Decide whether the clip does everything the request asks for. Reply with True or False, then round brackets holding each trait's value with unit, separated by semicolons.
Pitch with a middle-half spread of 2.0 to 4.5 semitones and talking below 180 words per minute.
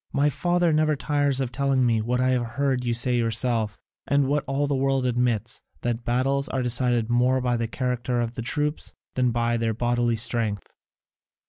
False (2.6 semitones; 190 wpm)